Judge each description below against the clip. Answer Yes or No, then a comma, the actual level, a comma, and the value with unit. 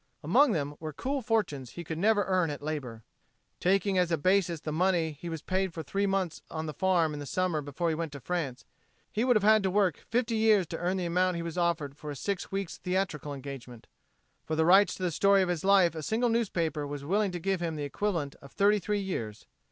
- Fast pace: Yes, fast, 235 wpm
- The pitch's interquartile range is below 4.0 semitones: No, average, 4.3 semitones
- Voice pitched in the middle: Yes, medium, 175 Hz